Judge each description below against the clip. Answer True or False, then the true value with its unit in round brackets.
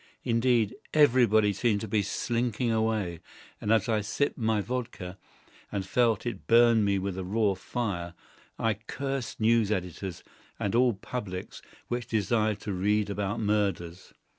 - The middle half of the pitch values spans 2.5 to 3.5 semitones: True (3.0 semitones)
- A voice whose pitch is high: False (110 Hz)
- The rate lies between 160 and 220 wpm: False (140 wpm)